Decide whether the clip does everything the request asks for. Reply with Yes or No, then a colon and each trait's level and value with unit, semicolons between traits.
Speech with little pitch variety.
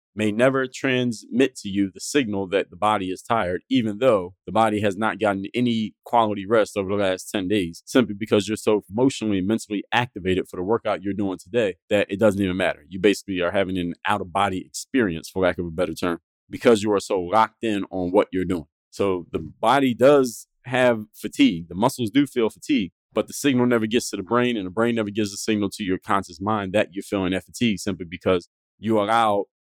No: average, 3.7 semitones